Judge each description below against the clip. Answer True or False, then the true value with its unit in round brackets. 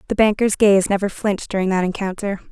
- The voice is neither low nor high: False (195 Hz)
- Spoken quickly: False (190 wpm)